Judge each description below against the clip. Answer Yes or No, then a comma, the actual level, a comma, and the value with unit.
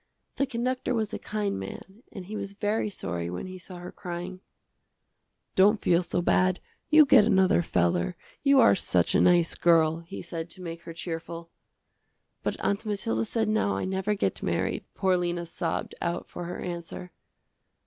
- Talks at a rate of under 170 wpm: No, average, 175 wpm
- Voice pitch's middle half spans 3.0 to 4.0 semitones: Yes, average, 3.4 semitones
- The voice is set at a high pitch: No, medium, 180 Hz